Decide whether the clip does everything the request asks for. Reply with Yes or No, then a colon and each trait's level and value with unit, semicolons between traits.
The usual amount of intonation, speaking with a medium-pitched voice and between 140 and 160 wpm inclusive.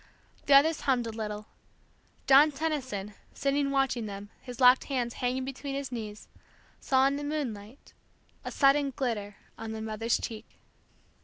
No: average, 4.0 semitones; very high, 255 Hz; average, 150 wpm